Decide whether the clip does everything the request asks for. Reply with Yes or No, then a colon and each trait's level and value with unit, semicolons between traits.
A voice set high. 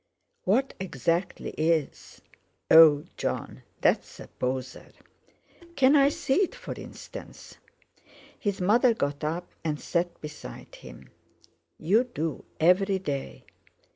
No: medium, 170 Hz